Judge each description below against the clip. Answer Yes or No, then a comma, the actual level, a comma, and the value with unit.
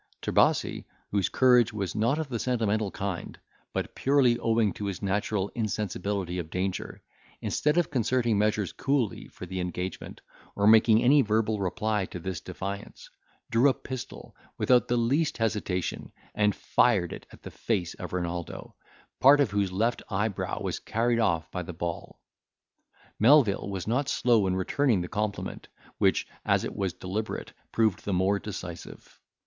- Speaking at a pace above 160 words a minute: No, average, 155 wpm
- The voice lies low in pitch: Yes, low, 105 Hz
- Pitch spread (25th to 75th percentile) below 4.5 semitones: Yes, average, 3.9 semitones